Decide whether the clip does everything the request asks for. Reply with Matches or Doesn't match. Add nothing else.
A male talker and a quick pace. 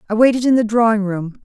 Doesn't match